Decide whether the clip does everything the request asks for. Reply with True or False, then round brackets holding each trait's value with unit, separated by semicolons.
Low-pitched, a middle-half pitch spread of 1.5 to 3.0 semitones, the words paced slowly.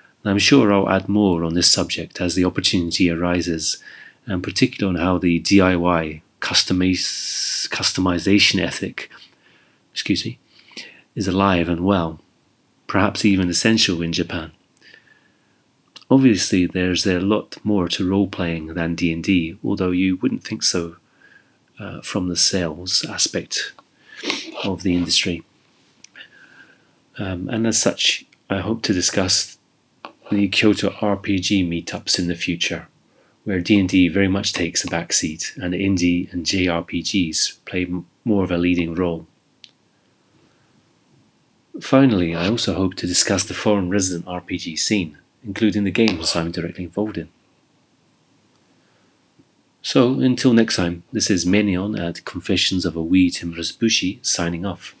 True (90 Hz; 2.4 semitones; 130 wpm)